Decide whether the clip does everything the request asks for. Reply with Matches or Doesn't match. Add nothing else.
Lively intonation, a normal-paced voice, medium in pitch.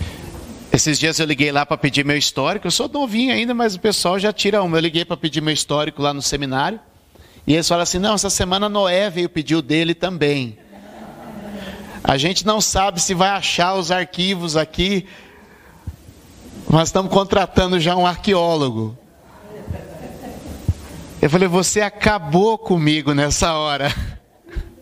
Doesn't match